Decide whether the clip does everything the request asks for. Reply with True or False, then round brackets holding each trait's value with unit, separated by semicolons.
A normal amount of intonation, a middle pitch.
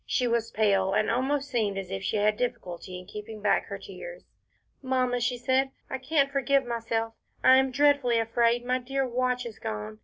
False (3.6 semitones; 240 Hz)